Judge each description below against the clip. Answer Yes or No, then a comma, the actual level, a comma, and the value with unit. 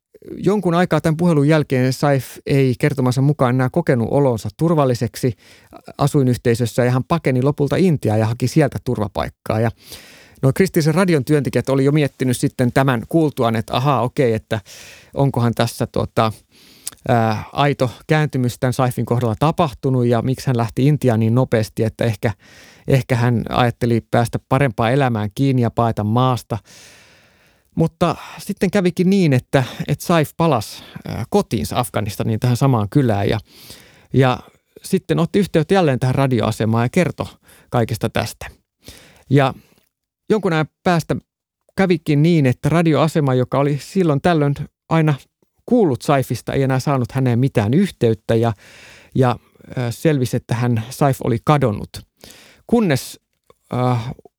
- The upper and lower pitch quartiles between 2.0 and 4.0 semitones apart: No, average, 4.4 semitones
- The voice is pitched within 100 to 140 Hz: Yes, low, 130 Hz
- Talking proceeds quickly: No, average, 135 wpm